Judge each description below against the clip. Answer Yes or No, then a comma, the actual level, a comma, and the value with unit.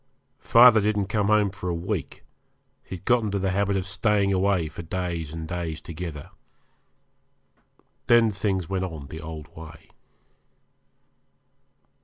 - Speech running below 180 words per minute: Yes, average, 140 wpm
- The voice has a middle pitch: No, very low, 95 Hz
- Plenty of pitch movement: No, average, 3.7 semitones